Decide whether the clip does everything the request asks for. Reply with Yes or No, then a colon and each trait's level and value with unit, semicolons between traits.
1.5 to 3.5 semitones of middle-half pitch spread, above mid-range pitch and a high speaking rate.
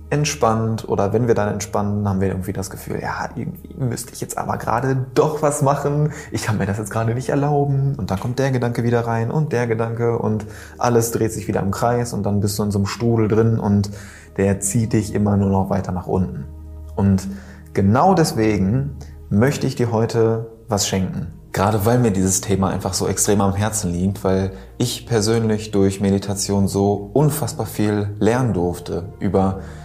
No: average, 3.1 semitones; low, 105 Hz; fast, 195 wpm